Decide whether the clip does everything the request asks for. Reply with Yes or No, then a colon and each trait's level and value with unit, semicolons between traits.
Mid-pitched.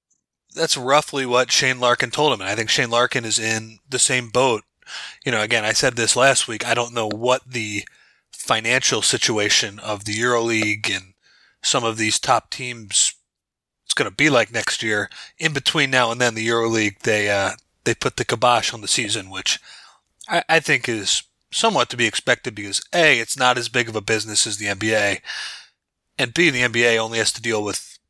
No: low, 115 Hz